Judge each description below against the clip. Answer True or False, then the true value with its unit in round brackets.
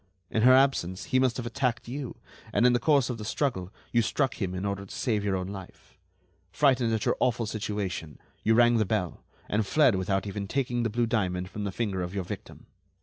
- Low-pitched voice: True (110 Hz)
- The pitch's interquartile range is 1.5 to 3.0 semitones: False (4.1 semitones)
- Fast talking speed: True (220 wpm)